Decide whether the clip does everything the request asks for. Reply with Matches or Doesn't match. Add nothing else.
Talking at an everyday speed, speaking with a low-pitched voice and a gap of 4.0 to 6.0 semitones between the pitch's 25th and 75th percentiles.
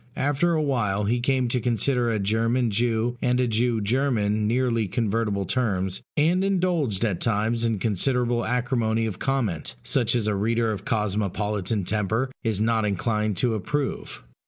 Doesn't match